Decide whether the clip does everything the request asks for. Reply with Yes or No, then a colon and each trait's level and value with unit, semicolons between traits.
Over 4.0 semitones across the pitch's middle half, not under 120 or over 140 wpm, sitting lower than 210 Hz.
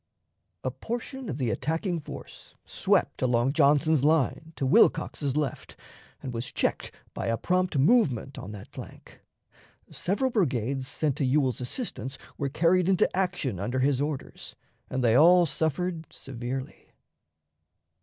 Yes: average, 4.9 semitones; slow, 135 wpm; medium, 140 Hz